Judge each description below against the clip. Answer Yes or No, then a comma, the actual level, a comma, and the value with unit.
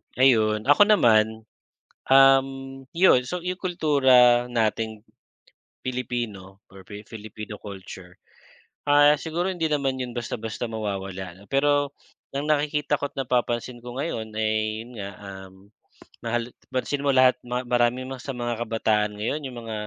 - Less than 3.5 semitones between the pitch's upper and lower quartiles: No, average, 4.1 semitones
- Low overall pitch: Yes, low, 120 Hz